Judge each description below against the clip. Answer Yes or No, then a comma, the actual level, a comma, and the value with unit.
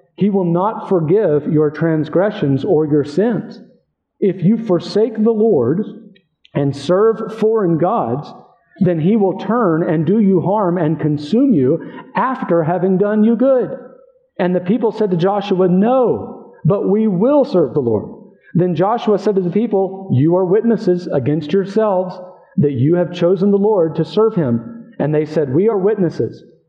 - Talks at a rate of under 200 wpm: Yes, average, 165 wpm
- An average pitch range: Yes, average, 4.0 semitones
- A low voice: No, high, 190 Hz